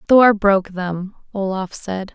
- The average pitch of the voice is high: Yes, high, 195 Hz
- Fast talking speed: No, average, 140 wpm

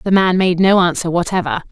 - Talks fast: Yes, fast, 210 wpm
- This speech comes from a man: No, female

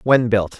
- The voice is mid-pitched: No, low, 110 Hz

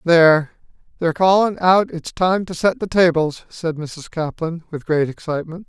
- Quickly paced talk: No, average, 170 wpm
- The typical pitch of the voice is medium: Yes, medium, 170 Hz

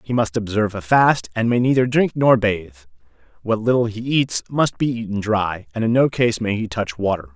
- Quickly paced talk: Yes, fast, 220 wpm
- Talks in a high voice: No, low, 110 Hz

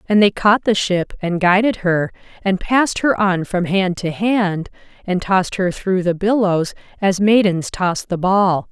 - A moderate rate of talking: Yes, average, 185 wpm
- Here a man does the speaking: No, female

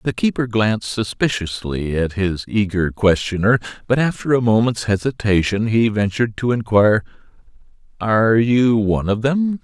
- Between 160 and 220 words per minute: No, slow, 135 wpm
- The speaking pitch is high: No, low, 110 Hz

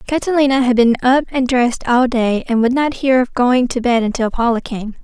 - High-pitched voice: Yes, very high, 250 Hz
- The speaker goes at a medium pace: No, fast, 225 wpm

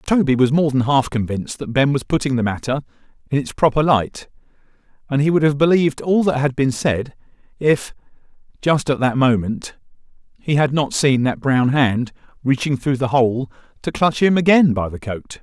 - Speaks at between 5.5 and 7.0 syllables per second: No, 5.1 syllables/s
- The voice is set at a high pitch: No, low, 135 Hz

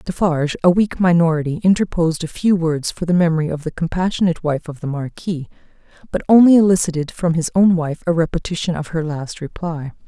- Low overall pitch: No, medium, 165 Hz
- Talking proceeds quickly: No, average, 185 wpm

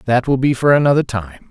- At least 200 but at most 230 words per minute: No, fast, 240 wpm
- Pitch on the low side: Yes, low, 125 Hz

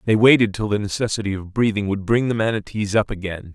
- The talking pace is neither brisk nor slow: No, fast, 220 wpm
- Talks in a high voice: No, low, 105 Hz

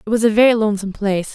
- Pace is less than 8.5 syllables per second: No, 8.9 syllables/s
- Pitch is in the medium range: No, high, 215 Hz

